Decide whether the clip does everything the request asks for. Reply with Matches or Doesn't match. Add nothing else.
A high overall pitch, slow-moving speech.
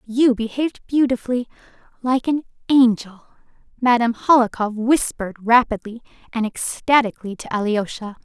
Matches